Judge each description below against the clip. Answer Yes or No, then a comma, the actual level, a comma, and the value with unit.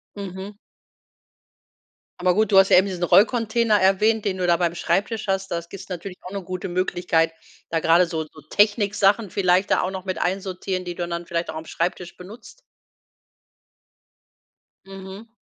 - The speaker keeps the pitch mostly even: Yes, narrow, 2.3 semitones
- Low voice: No, medium, 185 Hz